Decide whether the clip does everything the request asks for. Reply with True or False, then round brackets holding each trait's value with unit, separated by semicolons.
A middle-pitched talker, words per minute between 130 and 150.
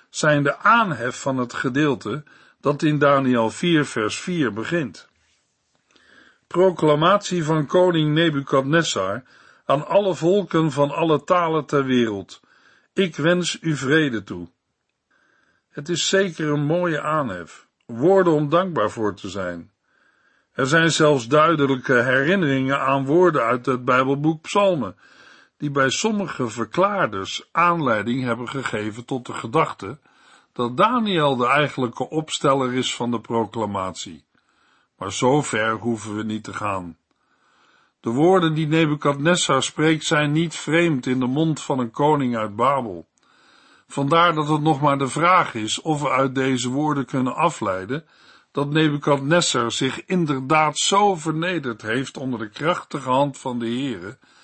True (145 Hz; 140 wpm)